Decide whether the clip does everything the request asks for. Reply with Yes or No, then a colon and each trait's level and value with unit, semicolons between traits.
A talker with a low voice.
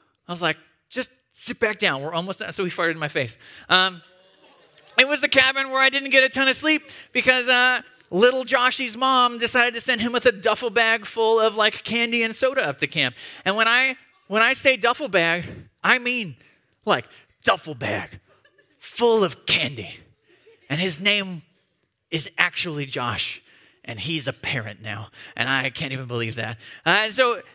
No: high, 215 Hz